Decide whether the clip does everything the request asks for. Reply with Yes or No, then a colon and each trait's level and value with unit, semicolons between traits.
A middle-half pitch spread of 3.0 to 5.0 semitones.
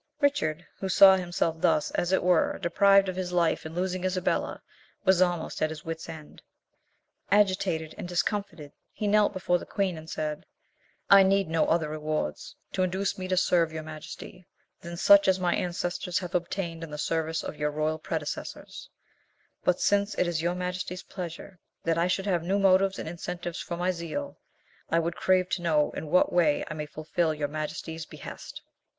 No: narrow, 2.6 semitones